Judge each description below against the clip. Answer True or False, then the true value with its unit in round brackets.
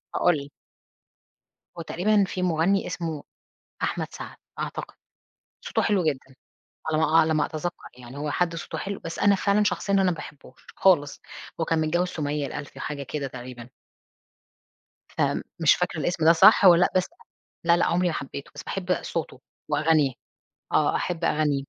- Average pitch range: True (3.6 semitones)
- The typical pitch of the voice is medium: True (165 Hz)